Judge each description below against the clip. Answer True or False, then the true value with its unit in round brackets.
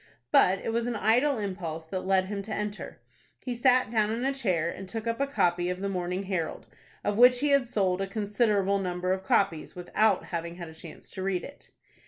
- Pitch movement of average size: True (4.2 semitones)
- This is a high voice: True (200 Hz)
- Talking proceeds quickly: True (220 wpm)